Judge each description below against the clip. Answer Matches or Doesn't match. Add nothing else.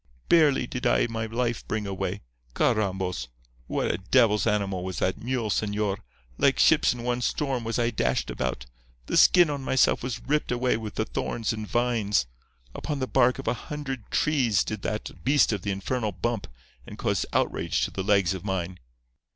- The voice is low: Matches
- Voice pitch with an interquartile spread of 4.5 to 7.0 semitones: Doesn't match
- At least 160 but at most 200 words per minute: Matches